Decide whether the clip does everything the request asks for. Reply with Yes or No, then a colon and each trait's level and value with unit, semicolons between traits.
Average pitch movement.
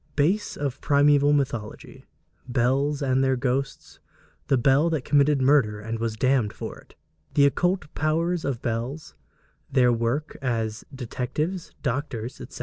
Yes: average, 3.4 semitones